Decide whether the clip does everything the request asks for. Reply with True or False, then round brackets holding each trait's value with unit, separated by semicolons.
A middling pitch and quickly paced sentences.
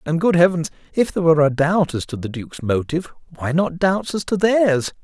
True (165 Hz; 225 wpm)